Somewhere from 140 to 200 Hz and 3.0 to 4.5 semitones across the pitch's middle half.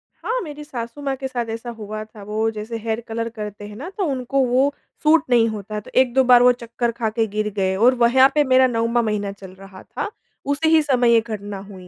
No: high, 235 Hz; average, 3.5 semitones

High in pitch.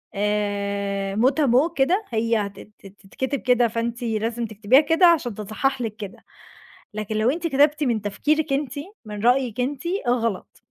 Yes: high, 235 Hz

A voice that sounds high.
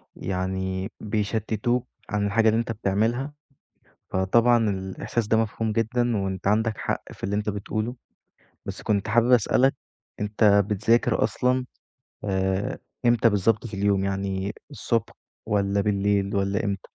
No: low, 105 Hz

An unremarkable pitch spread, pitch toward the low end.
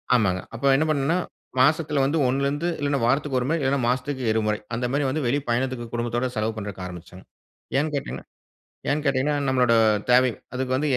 Yes: average, 3.3 semitones; low, 130 Hz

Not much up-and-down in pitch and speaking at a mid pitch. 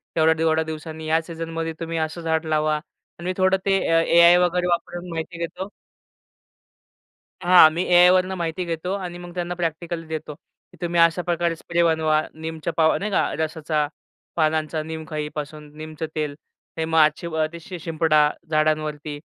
Yes: narrow, 1.8 semitones; medium, 165 Hz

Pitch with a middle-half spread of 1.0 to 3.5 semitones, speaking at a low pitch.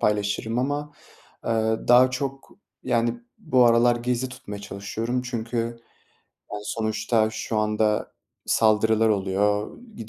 Yes: narrow, 2.5 semitones; low, 115 Hz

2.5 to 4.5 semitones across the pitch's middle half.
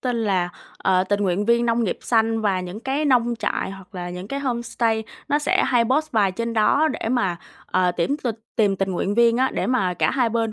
Yes: average, 4.1 semitones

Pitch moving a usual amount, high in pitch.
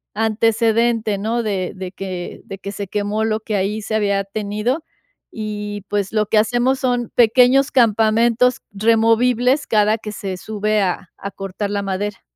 No: narrow, 2.2 semitones; high, 215 Hz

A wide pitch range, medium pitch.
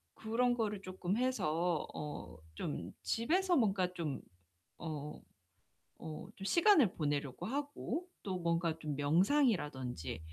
Yes: wide, 8.0 semitones; medium, 180 Hz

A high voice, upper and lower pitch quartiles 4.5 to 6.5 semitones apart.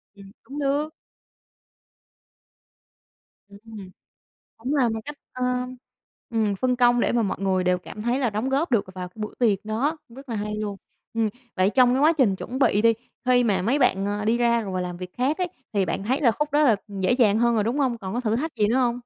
No: high, 230 Hz; average, 3.8 semitones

